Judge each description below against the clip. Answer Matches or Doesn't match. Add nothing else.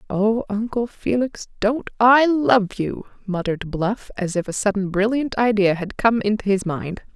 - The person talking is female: Matches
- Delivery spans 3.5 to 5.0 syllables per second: Matches